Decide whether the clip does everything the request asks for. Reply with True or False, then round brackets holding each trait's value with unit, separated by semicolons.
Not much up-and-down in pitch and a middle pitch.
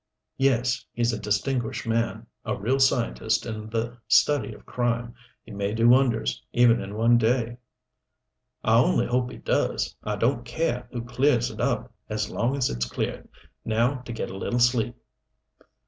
False (2.0 semitones; 120 Hz)